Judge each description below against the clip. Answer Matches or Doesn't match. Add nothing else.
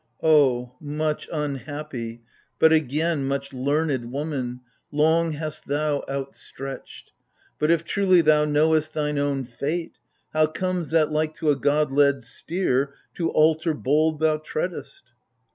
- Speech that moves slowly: Matches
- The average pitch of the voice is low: Doesn't match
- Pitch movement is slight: Matches